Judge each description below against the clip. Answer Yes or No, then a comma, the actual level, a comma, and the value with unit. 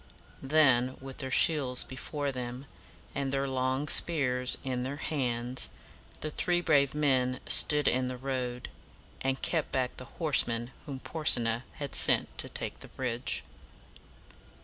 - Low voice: Yes, low, 130 Hz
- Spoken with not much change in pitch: Yes, narrow, 2.2 semitones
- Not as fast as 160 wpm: Yes, average, 140 wpm